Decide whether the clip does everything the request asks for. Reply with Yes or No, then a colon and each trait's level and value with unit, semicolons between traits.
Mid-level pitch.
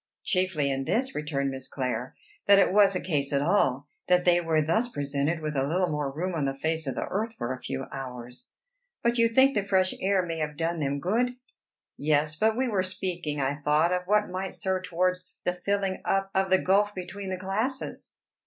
Yes: medium, 180 Hz